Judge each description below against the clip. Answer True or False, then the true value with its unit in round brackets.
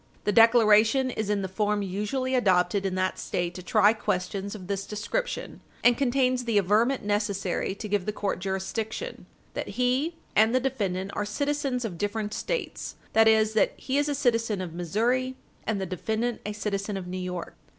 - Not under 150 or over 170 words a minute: False (180 wpm)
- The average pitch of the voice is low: False (210 Hz)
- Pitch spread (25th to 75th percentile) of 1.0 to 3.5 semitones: False (3.9 semitones)